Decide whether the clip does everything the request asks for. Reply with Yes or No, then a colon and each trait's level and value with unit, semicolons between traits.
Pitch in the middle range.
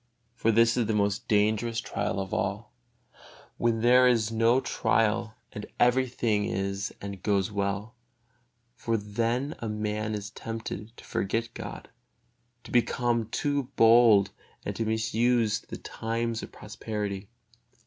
No: low, 110 Hz